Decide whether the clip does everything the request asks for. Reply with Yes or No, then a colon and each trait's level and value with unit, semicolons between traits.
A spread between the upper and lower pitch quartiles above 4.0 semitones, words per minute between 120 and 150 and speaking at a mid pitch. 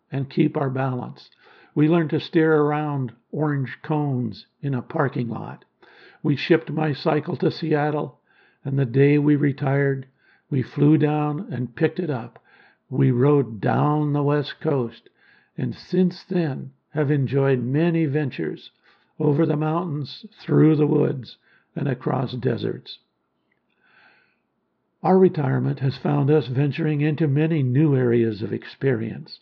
No: average, 2.7 semitones; slow, 135 wpm; medium, 145 Hz